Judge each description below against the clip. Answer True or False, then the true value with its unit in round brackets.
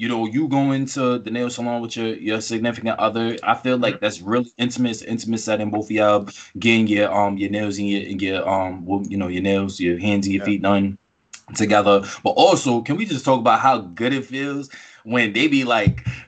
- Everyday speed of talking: False (220 wpm)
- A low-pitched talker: True (110 Hz)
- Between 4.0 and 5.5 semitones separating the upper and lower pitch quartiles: False (3.1 semitones)